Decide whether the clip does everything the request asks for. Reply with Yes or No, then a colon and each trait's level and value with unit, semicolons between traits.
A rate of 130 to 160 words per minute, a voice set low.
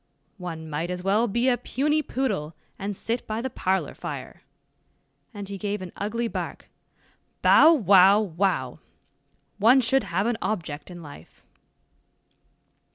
No: average, 140 wpm; high, 200 Hz